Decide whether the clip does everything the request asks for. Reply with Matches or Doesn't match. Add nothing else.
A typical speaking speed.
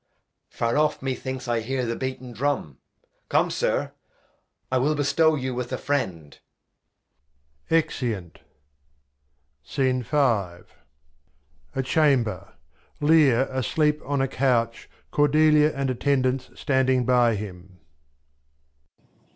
Doesn't match